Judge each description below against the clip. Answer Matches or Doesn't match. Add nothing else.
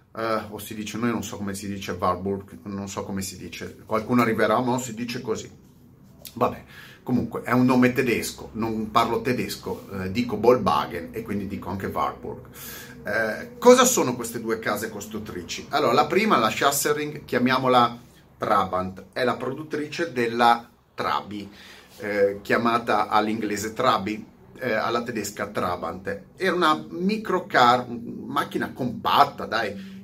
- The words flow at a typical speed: Matches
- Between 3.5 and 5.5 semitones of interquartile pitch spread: Matches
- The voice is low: Matches